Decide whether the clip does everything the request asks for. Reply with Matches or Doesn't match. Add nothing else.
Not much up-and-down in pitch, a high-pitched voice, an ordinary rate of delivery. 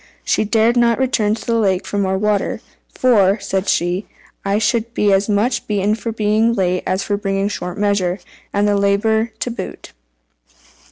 Matches